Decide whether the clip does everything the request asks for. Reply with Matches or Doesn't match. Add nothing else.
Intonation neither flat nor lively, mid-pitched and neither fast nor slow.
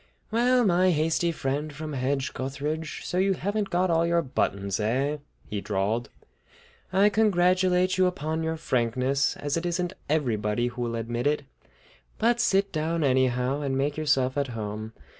Doesn't match